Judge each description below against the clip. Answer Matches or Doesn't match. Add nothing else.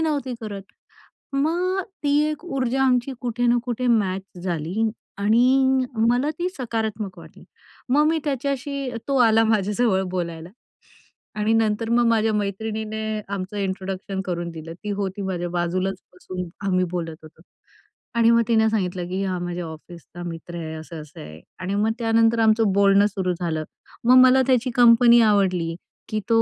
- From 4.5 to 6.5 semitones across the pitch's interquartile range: Matches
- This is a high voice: Matches